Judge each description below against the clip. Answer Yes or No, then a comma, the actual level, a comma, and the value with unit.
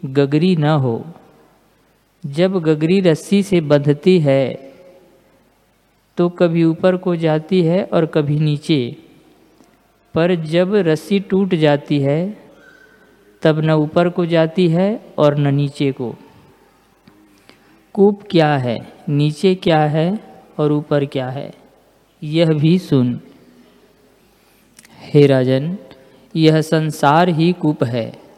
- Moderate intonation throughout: Yes, average, 3.7 semitones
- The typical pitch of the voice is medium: Yes, medium, 155 Hz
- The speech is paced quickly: No, average, 115 wpm